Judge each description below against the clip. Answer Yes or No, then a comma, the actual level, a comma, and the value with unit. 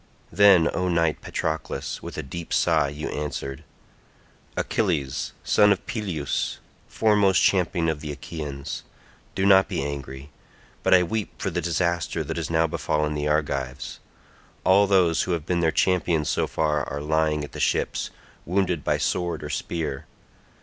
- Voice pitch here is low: Yes, very low, 80 Hz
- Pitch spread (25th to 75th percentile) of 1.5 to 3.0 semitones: No, average, 3.6 semitones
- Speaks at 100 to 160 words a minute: Yes, average, 155 wpm